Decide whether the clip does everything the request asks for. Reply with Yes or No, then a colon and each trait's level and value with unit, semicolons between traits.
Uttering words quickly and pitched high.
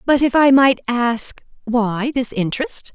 No: average, 145 wpm; very high, 250 Hz